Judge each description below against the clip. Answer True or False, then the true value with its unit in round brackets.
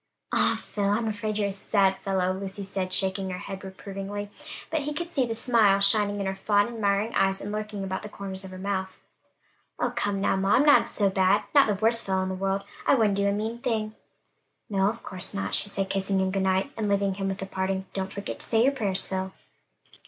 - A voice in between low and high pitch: False (200 Hz)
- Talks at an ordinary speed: False (235 wpm)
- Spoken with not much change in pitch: True (1.9 semitones)